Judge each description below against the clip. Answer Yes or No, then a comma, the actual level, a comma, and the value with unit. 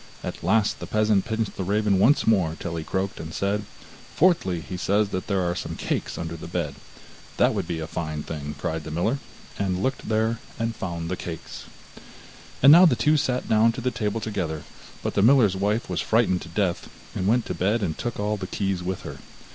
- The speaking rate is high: Yes, fast, 215 wpm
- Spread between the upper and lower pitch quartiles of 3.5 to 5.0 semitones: Yes, average, 4.4 semitones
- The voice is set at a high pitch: No, low, 100 Hz